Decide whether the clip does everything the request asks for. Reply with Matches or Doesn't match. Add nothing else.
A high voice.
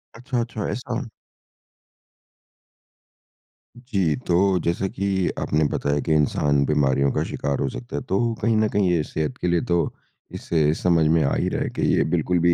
Doesn't match